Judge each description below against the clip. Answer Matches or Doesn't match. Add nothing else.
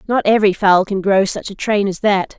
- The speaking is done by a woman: Matches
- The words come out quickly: Matches